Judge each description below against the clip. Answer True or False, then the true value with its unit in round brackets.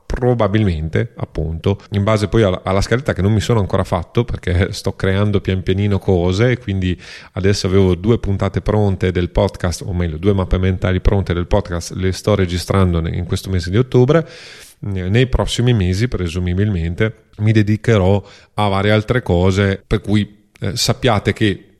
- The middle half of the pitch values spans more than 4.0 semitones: False (2.6 semitones)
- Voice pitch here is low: True (100 Hz)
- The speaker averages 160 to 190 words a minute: True (165 wpm)